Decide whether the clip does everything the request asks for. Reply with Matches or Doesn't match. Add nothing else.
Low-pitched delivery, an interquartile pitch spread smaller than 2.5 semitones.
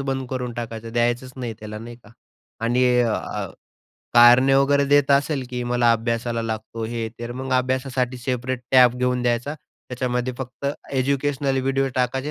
Matches